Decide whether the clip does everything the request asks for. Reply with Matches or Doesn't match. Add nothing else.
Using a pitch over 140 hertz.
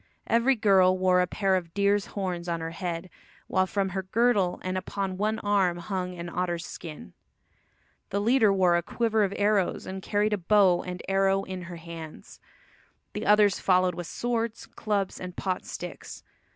Matches